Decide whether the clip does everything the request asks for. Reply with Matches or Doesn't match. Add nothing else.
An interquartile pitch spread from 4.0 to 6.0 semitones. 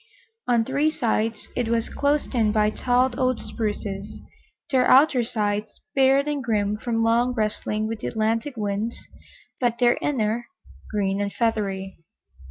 Doesn't match